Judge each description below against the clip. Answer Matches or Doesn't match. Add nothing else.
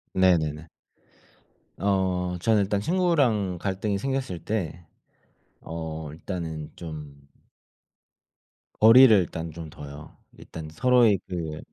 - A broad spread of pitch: Doesn't match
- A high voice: Doesn't match